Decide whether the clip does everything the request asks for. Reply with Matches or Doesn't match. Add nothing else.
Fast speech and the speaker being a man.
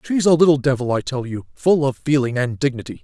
Matches